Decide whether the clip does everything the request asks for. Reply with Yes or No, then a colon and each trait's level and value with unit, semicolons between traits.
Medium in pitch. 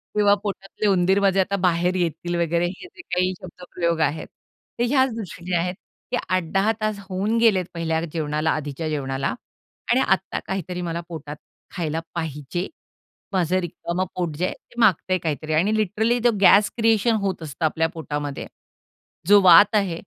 Yes: medium, 180 Hz